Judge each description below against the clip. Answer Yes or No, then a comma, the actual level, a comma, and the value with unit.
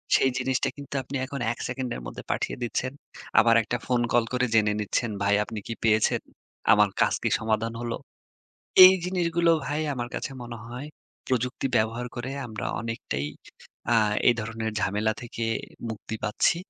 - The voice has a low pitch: Yes, low, 120 Hz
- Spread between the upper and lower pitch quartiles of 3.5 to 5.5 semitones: No, average, 2.7 semitones